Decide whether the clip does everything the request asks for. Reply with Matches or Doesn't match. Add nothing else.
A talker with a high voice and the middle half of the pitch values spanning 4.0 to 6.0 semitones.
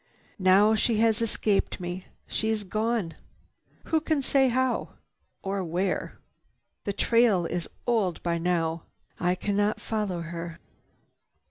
Matches